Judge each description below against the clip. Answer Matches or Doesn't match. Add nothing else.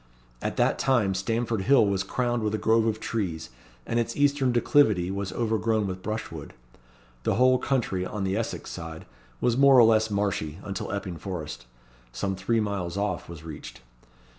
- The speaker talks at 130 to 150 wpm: Doesn't match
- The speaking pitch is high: Doesn't match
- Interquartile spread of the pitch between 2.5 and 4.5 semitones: Matches